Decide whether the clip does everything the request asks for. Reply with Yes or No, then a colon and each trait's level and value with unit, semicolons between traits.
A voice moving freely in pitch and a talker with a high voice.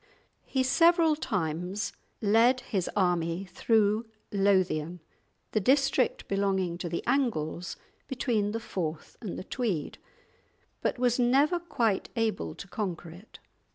Yes: wide, 5.7 semitones; high, 205 Hz